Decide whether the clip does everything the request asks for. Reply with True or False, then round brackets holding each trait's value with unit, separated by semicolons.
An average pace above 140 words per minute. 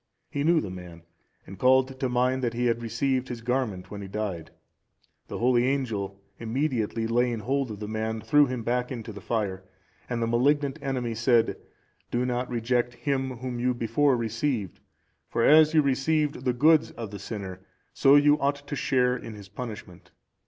True (180 wpm)